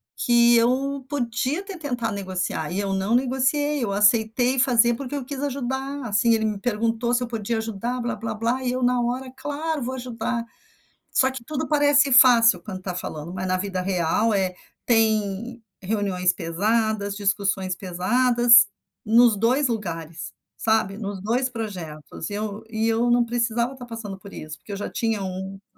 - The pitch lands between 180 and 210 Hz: No, high, 230 Hz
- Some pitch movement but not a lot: Yes, average, 3.9 semitones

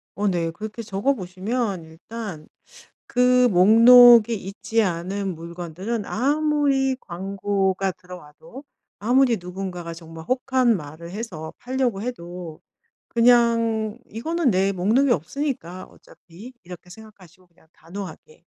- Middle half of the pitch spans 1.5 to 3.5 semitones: No, average, 5.3 semitones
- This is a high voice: Yes, high, 205 Hz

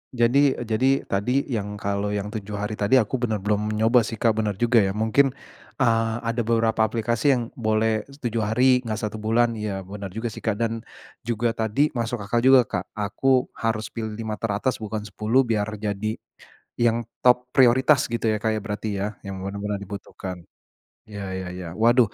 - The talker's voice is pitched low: Yes, low, 110 Hz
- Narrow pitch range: Yes, narrow, 2.3 semitones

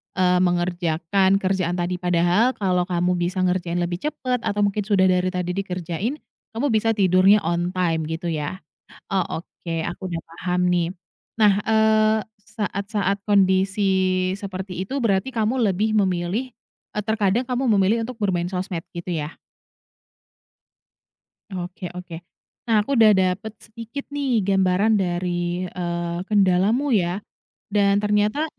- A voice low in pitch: No, high, 190 Hz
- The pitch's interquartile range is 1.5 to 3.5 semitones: Yes, average, 3.0 semitones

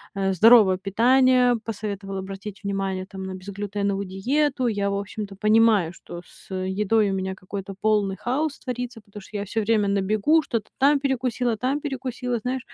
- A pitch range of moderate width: Yes, average, 4.1 semitones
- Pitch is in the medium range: No, high, 210 Hz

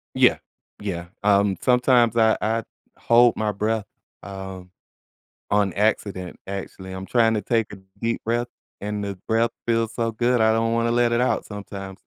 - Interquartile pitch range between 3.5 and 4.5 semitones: No, average, 2.8 semitones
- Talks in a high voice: No, low, 110 Hz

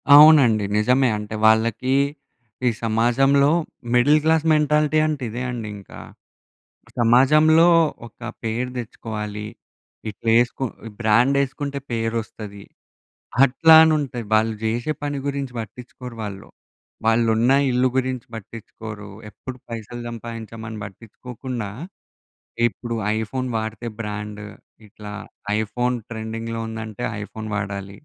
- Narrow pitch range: No, average, 3.0 semitones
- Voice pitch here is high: No, low, 115 Hz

